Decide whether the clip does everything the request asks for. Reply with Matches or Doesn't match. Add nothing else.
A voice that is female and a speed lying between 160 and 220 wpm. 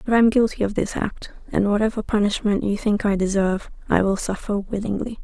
Matches